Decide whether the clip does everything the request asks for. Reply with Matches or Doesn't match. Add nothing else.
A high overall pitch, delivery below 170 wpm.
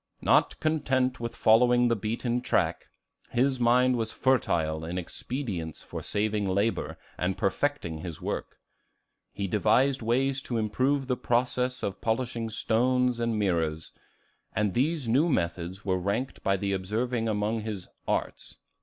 Doesn't match